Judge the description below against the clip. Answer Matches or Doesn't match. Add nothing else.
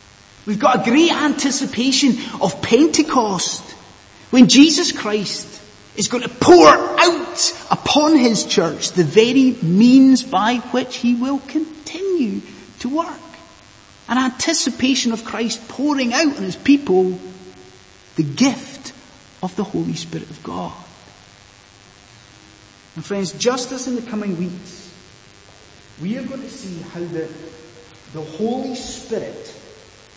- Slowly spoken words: Matches